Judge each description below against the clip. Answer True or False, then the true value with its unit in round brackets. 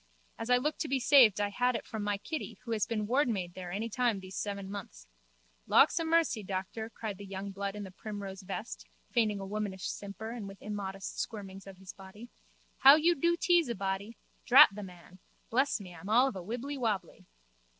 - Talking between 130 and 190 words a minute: False (200 wpm)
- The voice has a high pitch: True (210 Hz)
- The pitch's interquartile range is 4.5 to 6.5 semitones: False (4.0 semitones)